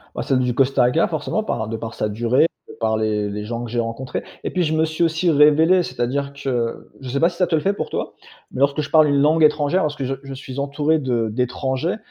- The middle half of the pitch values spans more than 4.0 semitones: Yes, average, 4.4 semitones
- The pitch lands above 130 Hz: Yes, medium, 140 Hz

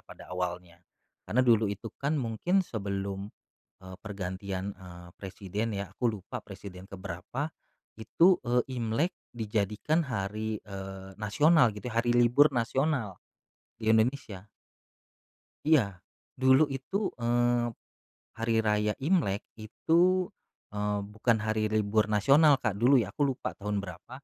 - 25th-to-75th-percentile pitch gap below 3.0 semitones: No, average, 3.9 semitones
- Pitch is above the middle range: No, low, 110 Hz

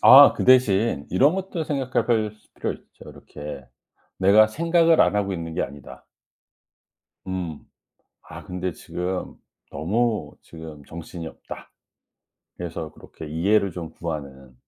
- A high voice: No, very low, 95 Hz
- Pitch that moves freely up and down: Yes, wide, 6.4 semitones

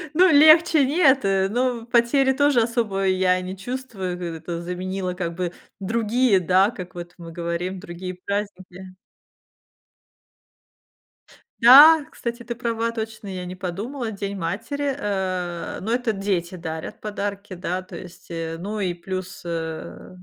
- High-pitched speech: Yes, high, 195 Hz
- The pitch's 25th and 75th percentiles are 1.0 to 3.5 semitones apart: No, average, 4.6 semitones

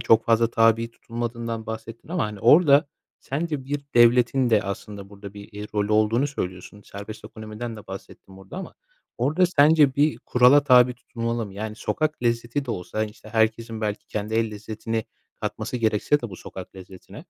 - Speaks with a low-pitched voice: Yes, low, 115 Hz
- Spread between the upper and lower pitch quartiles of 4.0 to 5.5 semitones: No, average, 2.8 semitones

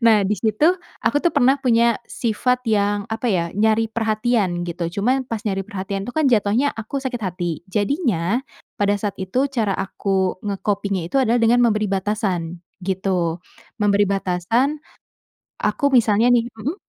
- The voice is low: No, high, 215 Hz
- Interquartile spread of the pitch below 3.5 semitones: Yes, average, 3.1 semitones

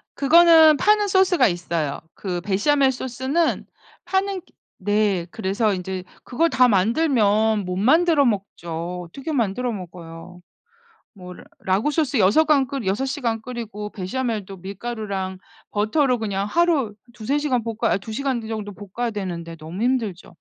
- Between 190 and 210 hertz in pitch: No, high, 220 Hz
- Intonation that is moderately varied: No, wide, 6.1 semitones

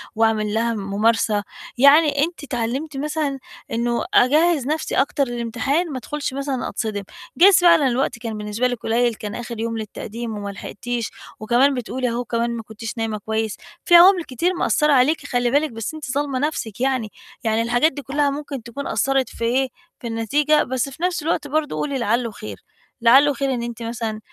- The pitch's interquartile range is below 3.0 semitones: No, average, 4.1 semitones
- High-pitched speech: Yes, very high, 250 Hz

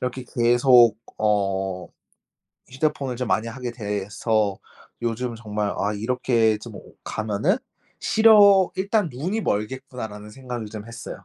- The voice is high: No, low, 115 Hz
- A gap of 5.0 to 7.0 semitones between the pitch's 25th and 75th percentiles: No, average, 3.5 semitones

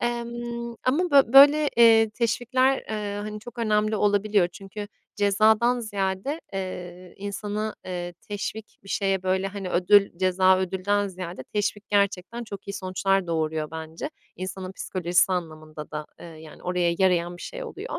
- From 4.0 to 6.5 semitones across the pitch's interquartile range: No, average, 3.3 semitones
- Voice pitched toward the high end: Yes, high, 200 Hz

